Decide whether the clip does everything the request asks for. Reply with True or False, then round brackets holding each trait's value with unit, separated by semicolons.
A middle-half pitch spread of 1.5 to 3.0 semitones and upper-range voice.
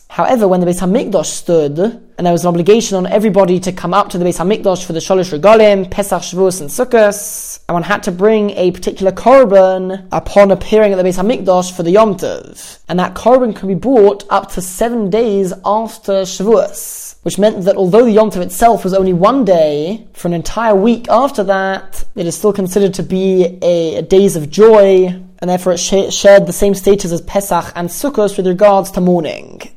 True (2.6 semitones; 195 Hz)